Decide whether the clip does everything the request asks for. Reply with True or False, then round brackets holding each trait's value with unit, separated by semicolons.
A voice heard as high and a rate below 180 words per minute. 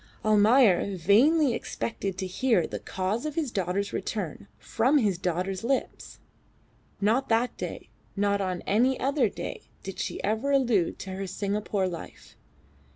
True (205 Hz; 150 wpm)